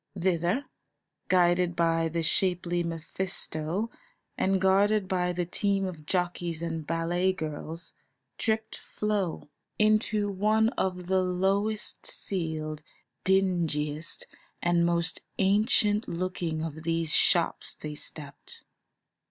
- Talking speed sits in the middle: No, slow, 105 wpm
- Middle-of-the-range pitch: Yes, medium, 180 Hz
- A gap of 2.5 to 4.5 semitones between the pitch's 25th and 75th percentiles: Yes, average, 2.8 semitones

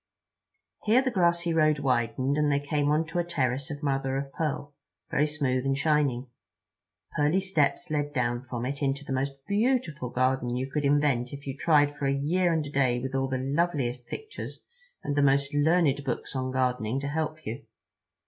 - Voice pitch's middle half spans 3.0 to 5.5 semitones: No, narrow, 2.6 semitones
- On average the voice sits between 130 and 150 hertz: Yes, medium, 140 Hz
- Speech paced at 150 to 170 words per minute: No, average, 185 wpm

